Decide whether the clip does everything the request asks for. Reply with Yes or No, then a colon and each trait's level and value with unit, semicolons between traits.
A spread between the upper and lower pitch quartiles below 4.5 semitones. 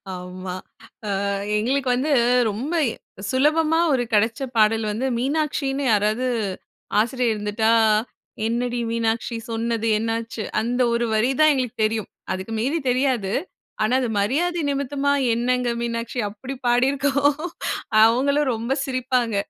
Yes: average, 3.3 semitones